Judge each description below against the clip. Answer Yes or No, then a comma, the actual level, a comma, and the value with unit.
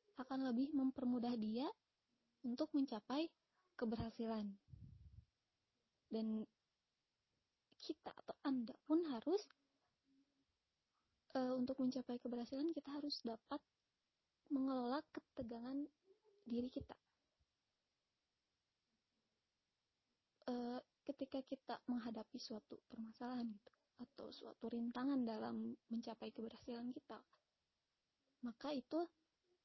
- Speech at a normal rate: No, slow, 80 wpm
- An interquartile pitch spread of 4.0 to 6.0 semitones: No, average, 3.5 semitones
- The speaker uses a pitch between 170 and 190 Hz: No, very high, 255 Hz